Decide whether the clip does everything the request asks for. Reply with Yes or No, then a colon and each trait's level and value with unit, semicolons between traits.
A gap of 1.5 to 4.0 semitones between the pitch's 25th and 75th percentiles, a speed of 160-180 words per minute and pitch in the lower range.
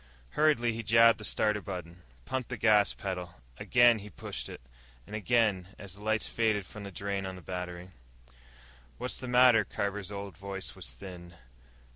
Yes: average, 3.4 semitones; average, 170 wpm; low, 100 Hz